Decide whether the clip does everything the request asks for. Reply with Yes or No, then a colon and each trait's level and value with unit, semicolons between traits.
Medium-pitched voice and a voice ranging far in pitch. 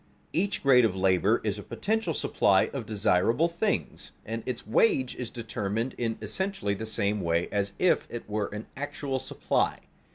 No: low, 115 Hz; wide, 6.2 semitones